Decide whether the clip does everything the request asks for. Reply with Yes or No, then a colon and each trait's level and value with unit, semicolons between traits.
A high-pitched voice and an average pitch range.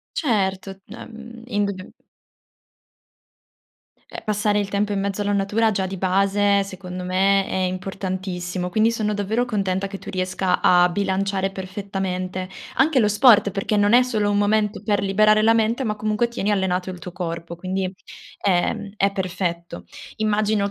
No: high, 200 Hz; narrow, 2.2 semitones